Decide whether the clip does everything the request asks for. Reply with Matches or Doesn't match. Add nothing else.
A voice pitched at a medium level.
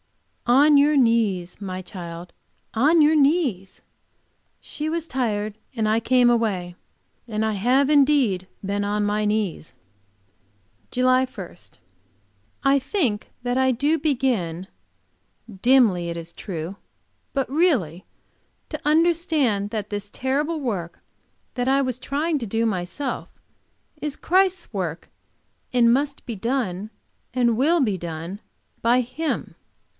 Doesn't match